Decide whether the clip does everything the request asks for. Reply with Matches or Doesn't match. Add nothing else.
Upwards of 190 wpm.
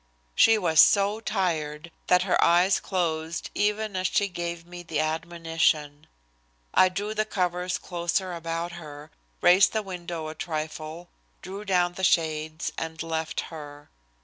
Doesn't match